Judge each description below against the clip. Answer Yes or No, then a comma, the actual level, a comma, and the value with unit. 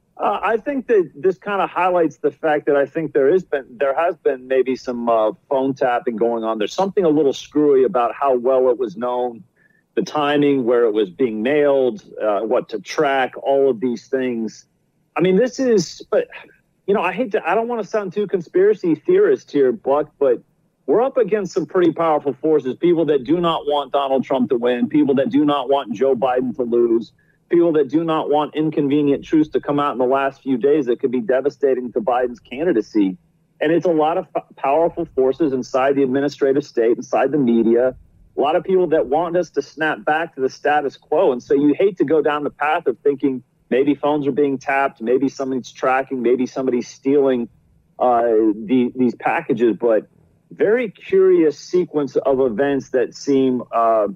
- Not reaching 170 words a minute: No, fast, 205 wpm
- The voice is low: No, medium, 145 Hz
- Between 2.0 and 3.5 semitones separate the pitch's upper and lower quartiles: No, average, 4.8 semitones